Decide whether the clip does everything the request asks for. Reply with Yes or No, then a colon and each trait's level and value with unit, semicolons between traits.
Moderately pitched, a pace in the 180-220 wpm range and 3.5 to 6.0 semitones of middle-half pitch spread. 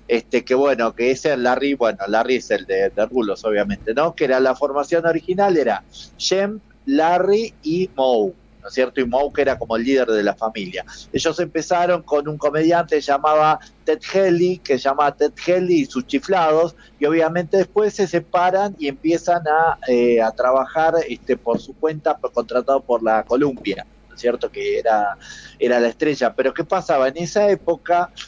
Yes: medium, 155 Hz; average, 185 wpm; wide, 5.5 semitones